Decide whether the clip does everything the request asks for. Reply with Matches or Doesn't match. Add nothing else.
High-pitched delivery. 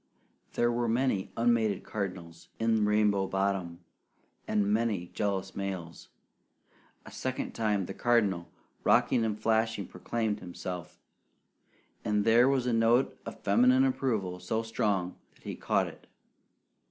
Doesn't match